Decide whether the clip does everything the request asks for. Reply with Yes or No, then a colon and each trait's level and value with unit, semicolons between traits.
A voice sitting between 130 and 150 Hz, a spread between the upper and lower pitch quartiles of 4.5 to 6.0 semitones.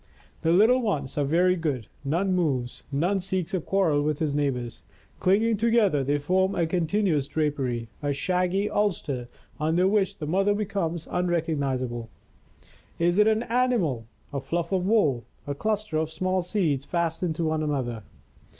No: medium, 170 Hz; average, 5.1 semitones